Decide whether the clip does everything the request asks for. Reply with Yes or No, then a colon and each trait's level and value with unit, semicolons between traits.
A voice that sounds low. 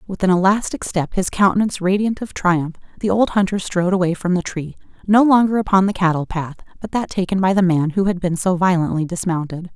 No: medium, 185 Hz